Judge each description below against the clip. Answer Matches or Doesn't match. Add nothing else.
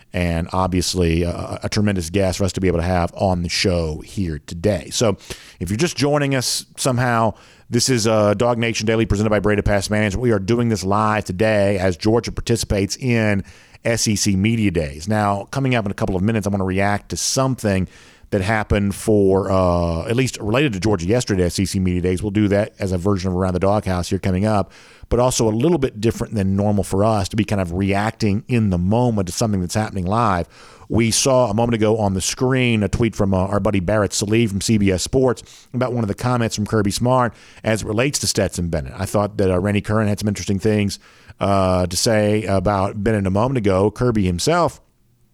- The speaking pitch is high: Doesn't match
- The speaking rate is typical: Doesn't match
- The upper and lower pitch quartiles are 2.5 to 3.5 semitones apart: Matches